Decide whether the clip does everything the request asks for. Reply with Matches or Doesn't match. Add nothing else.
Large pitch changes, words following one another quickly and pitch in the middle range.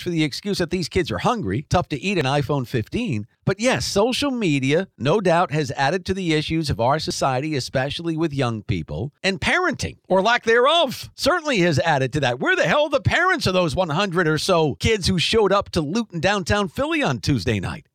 Matches